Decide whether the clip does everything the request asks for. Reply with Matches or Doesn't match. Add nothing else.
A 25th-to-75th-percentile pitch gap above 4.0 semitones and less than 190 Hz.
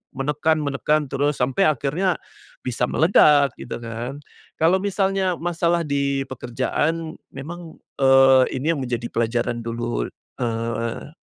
Matches